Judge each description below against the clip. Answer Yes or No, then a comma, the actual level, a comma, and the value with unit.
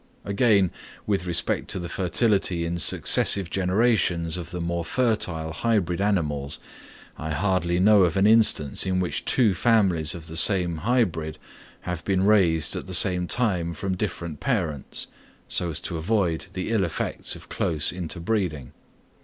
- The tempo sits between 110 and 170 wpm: Yes, average, 155 wpm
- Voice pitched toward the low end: Yes, very low, 90 Hz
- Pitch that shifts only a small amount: No, average, 3.4 semitones